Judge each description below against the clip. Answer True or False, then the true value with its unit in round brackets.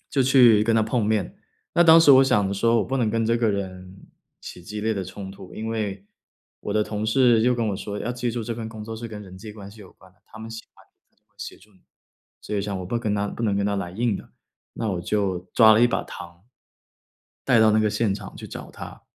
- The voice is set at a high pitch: False (110 Hz)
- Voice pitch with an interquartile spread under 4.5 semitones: True (2.5 semitones)